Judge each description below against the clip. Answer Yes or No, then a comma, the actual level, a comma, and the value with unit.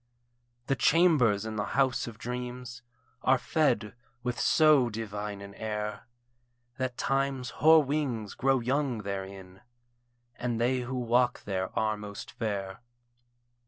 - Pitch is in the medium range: No, low, 120 Hz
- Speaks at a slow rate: Yes, slow, 125 wpm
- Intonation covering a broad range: No, average, 3.8 semitones